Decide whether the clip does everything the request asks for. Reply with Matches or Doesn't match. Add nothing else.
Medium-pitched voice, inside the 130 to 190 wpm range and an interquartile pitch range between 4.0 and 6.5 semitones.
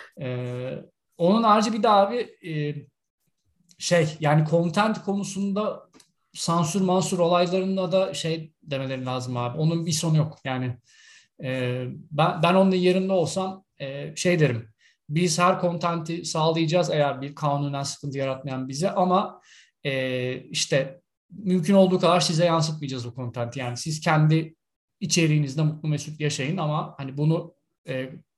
Matches